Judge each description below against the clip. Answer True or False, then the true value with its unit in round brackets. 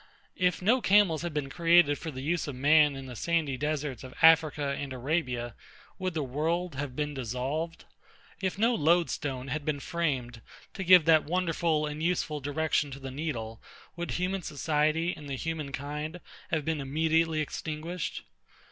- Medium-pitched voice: True (155 Hz)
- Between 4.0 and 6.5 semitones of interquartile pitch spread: False (3.2 semitones)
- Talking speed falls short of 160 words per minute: False (165 wpm)